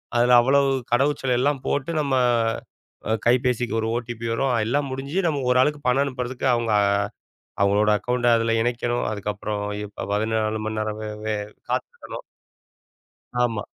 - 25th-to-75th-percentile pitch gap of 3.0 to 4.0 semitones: Yes, average, 3.4 semitones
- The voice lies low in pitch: Yes, low, 120 Hz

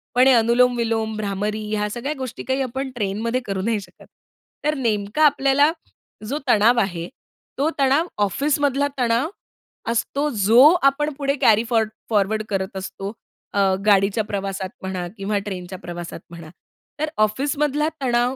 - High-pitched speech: Yes, high, 230 Hz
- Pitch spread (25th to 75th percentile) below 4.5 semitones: No, average, 5.1 semitones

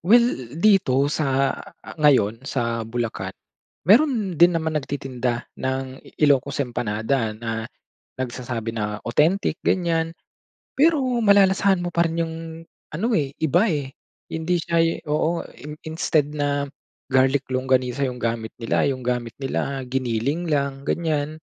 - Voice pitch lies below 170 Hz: Yes, medium, 140 Hz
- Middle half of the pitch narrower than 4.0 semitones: No, average, 4.8 semitones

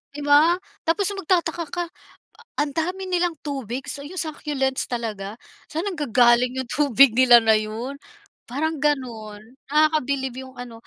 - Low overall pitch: No, very high, 275 Hz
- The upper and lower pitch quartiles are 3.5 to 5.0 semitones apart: Yes, average, 4.3 semitones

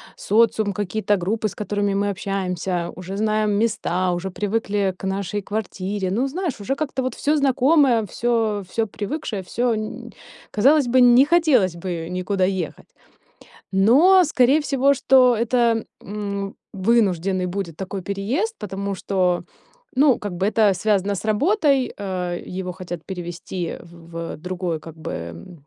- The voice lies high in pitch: Yes, high, 205 Hz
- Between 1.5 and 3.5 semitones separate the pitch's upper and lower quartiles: No, average, 4.5 semitones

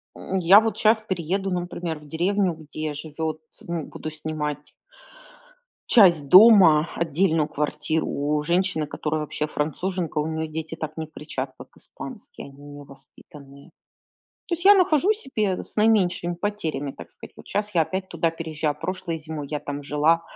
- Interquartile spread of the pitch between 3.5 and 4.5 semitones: Yes, average, 3.8 semitones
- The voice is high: No, medium, 160 Hz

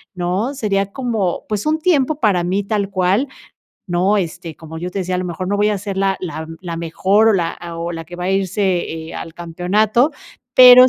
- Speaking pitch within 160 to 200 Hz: Yes, high, 190 Hz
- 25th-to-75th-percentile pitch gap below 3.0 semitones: No, average, 3.4 semitones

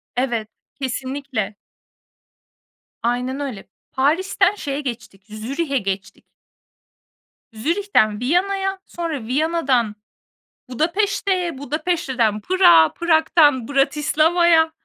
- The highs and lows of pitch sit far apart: Yes, wide, 5.9 semitones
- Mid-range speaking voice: No, very high, 285 Hz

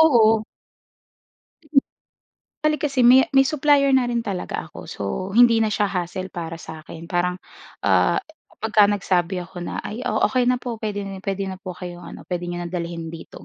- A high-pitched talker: Yes, high, 200 Hz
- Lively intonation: Yes, wide, 5.7 semitones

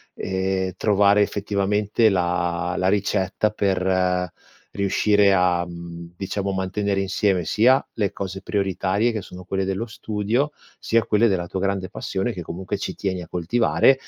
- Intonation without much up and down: Yes, narrow, 2.0 semitones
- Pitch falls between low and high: No, very low, 95 Hz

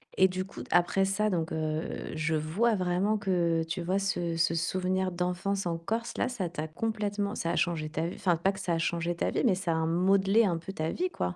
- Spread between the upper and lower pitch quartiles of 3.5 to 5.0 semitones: No, average, 2.9 semitones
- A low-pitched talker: No, medium, 180 Hz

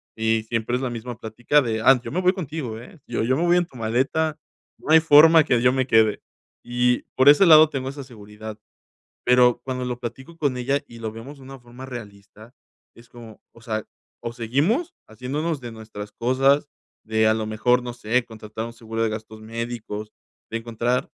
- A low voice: Yes, low, 120 Hz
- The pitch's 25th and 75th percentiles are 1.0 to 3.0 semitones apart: No, average, 3.4 semitones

